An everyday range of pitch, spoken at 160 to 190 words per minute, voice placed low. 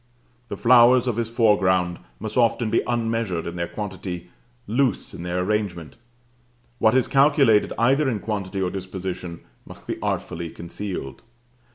No: average, 4.6 semitones; average, 145 wpm; low, 105 Hz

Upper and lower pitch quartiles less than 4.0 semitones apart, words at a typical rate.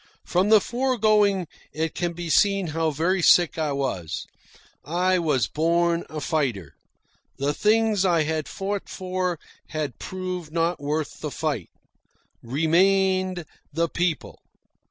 No: average, 3.4 semitones; slow, 130 wpm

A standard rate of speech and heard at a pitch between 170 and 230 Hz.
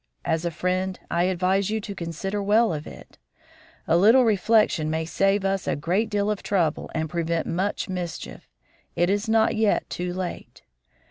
Yes: average, 175 wpm; high, 190 Hz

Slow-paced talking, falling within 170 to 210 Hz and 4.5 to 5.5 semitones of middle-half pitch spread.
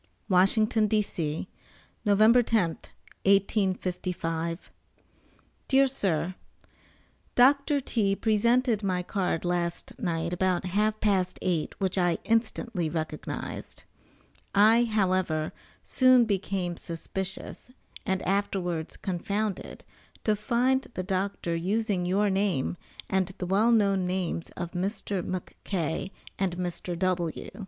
No: slow, 105 wpm; high, 190 Hz; average, 3.3 semitones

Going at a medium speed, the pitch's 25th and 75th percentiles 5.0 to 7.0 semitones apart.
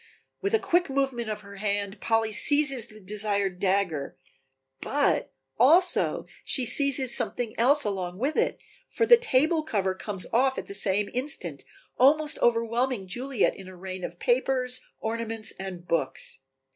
Yes: average, 150 wpm; average, 5.3 semitones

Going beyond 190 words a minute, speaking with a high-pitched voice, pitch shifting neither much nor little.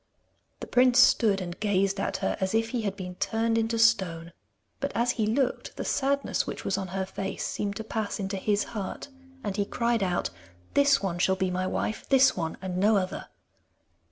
Yes: average, 200 wpm; high, 205 Hz; average, 3.3 semitones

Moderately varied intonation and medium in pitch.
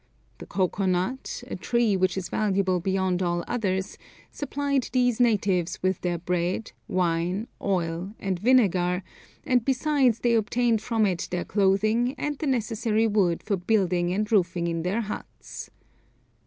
No: average, 4.5 semitones; high, 200 Hz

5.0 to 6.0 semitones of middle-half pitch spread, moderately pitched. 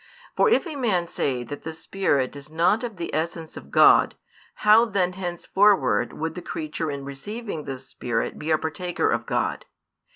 Yes: wide, 5.4 semitones; medium, 165 Hz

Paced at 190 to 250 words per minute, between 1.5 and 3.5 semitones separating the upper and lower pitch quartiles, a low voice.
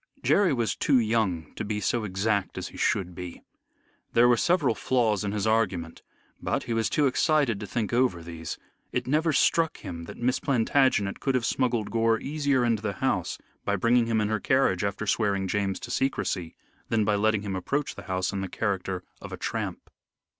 No: average, 195 wpm; average, 4.2 semitones; low, 110 Hz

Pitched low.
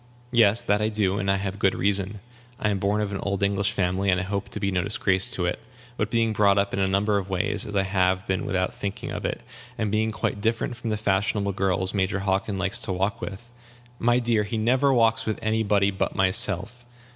Yes: low, 100 Hz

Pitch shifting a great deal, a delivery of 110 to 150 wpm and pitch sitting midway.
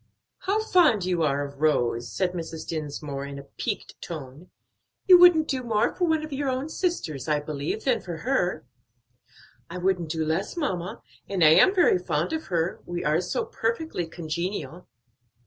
No: wide, 9.0 semitones; average, 175 wpm; medium, 175 Hz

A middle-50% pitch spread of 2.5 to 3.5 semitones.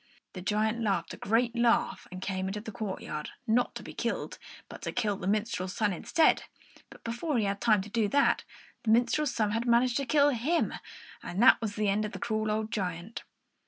Yes: average, 2.9 semitones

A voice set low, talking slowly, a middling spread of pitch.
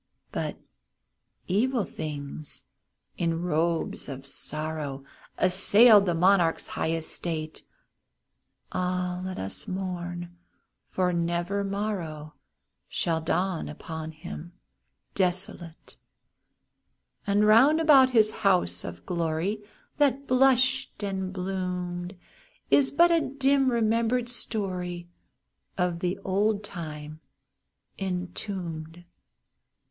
No: medium, 180 Hz; slow, 95 wpm; average, 4.3 semitones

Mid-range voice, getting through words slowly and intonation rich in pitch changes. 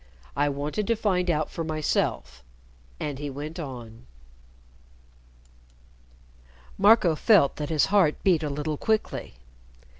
No: medium, 155 Hz; slow, 120 wpm; average, 4.0 semitones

